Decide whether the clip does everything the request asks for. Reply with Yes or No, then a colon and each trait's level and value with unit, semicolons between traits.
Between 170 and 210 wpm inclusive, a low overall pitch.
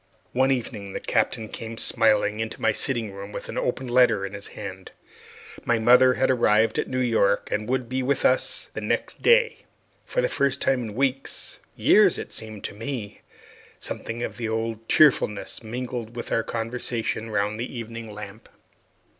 Yes: average, 175 wpm; low, 115 Hz